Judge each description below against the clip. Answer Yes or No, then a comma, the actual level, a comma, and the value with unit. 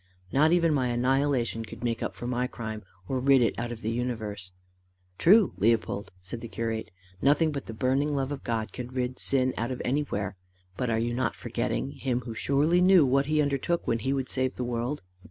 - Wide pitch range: No, average, 3.2 semitones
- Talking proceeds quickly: Yes, fast, 210 wpm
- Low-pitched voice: Yes, low, 125 Hz